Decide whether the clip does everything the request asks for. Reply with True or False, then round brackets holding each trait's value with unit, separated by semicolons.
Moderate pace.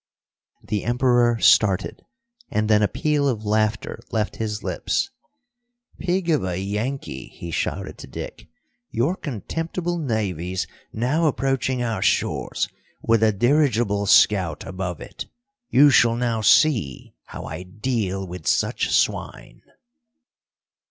False (125 wpm)